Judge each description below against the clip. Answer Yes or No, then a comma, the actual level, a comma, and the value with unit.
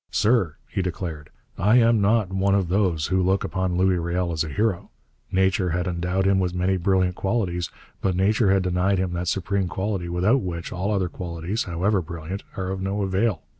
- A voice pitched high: No, very low, 95 Hz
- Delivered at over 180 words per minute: Yes, average, 195 wpm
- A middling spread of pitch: No, narrow, 1.9 semitones